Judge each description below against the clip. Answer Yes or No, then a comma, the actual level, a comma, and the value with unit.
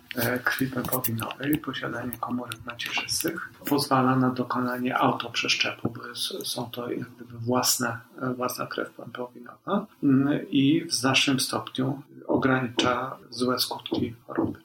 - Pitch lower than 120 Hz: No, low, 125 Hz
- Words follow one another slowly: Yes, slow, 100 wpm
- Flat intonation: Yes, narrow, 1.8 semitones